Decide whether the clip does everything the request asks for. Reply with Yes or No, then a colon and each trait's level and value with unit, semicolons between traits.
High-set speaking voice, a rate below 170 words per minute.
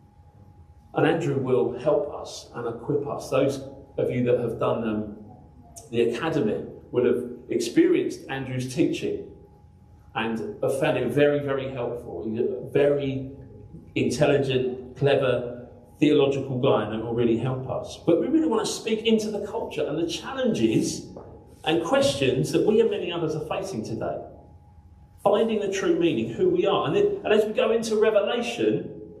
No: medium, 140 Hz; average, 160 wpm